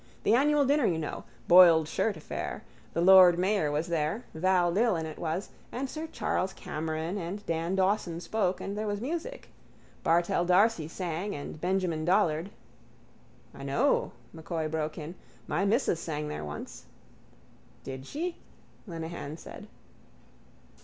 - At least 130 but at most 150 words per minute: Yes, average, 140 wpm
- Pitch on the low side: No, medium, 175 Hz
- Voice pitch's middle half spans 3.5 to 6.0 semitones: Yes, average, 4.3 semitones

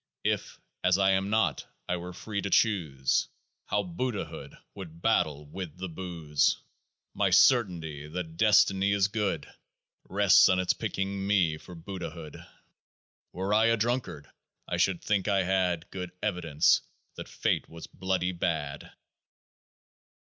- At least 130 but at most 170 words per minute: Yes, average, 145 wpm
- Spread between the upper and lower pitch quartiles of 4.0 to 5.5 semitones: No, average, 3.3 semitones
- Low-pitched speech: Yes, very low, 90 Hz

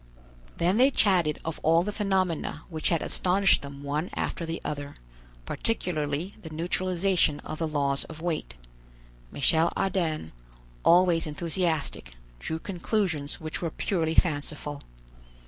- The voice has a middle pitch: Yes, medium, 165 Hz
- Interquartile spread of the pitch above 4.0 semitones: No, average, 3.3 semitones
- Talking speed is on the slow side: Yes, slow, 130 wpm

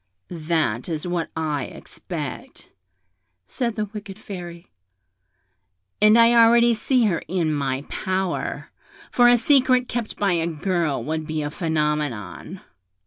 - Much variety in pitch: Yes, wide, 5.9 semitones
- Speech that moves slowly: Yes, slow, 130 wpm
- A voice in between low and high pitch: Yes, medium, 175 Hz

